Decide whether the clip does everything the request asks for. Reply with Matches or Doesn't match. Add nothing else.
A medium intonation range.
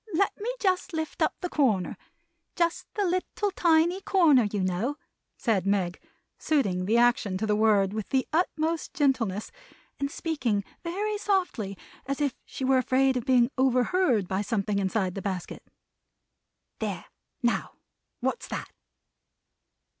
Doesn't match